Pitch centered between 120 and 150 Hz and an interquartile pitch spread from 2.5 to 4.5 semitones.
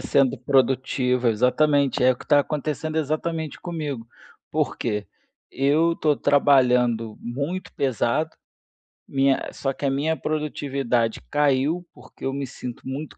Yes: medium, 140 Hz; average, 3.2 semitones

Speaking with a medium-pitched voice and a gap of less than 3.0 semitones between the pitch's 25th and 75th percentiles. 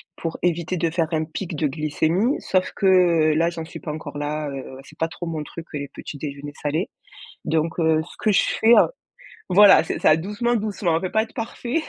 No: medium, 165 Hz; average, 3.3 semitones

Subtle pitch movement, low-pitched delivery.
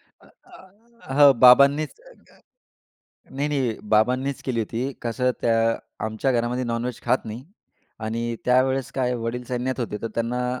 Yes: narrow, 2.3 semitones; low, 125 Hz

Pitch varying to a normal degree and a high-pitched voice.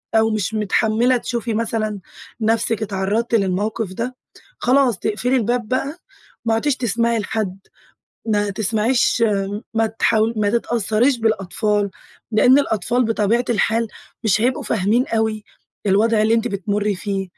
No: narrow, 2.1 semitones; high, 220 Hz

